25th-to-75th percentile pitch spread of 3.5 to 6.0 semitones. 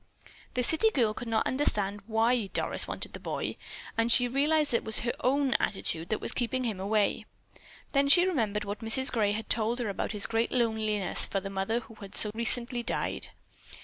No: average, 3.0 semitones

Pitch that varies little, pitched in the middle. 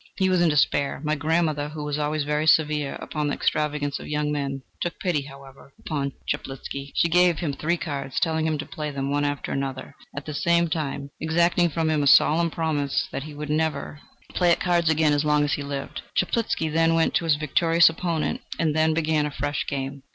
Yes: narrow, 2.1 semitones; medium, 150 Hz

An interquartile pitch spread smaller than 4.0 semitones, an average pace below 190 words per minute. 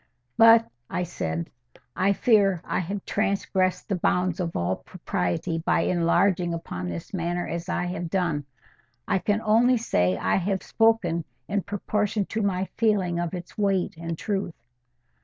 Yes: average, 3.0 semitones; average, 155 wpm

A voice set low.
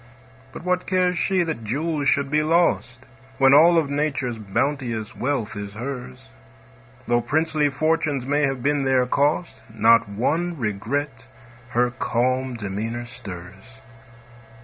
Yes: low, 130 Hz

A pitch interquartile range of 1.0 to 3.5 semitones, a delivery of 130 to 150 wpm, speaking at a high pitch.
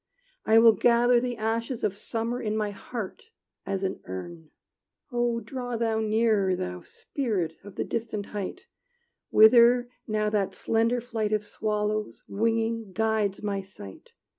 Yes: narrow, 2.4 semitones; average, 140 wpm; high, 220 Hz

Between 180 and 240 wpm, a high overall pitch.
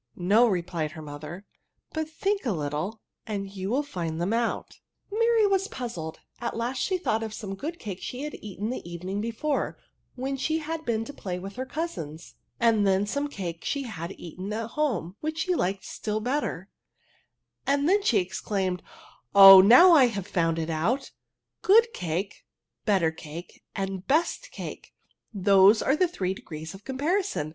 Yes: average, 190 wpm; high, 210 Hz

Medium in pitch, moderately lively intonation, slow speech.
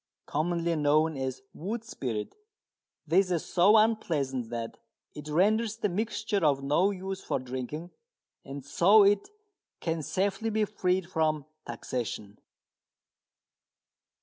No: medium, 170 Hz; wide, 6.2 semitones; slow, 120 wpm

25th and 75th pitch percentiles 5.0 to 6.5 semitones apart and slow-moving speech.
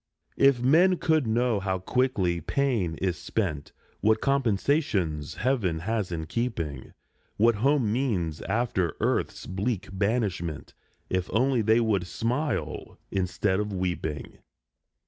Yes: wide, 5.5 semitones; slow, 125 wpm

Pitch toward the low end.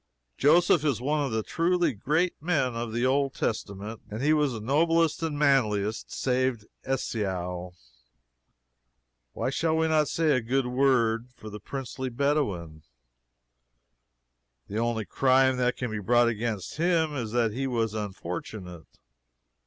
Yes: low, 125 Hz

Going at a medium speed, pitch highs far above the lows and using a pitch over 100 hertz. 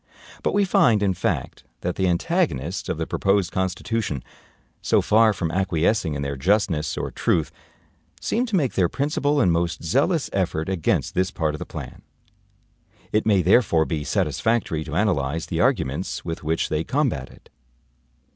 No: average, 165 wpm; wide, 5.7 semitones; very low, 95 Hz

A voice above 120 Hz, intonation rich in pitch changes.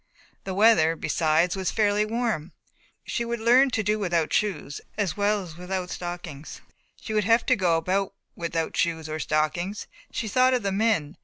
No: high, 190 Hz; average, 4.6 semitones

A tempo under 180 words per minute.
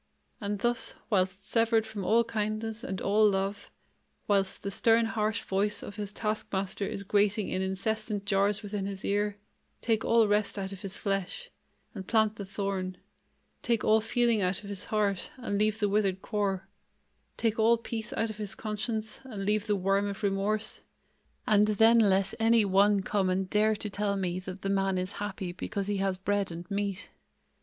No: average, 185 wpm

